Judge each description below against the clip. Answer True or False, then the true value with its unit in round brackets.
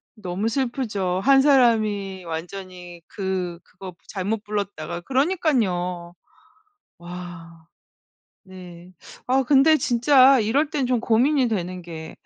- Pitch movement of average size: False (6.3 semitones)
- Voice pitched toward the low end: False (200 Hz)